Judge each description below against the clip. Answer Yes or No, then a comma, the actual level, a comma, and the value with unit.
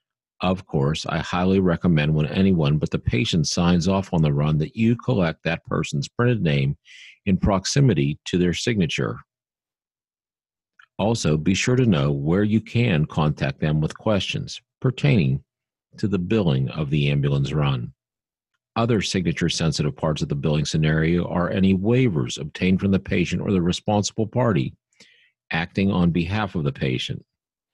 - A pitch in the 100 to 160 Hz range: No, very low, 90 Hz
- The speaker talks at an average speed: Yes, average, 155 wpm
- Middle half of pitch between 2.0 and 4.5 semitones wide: No, wide, 5.6 semitones